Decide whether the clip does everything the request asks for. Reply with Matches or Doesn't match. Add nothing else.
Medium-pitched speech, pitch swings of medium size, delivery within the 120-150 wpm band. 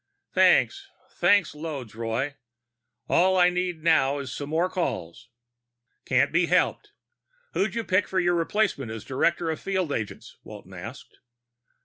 Doesn't match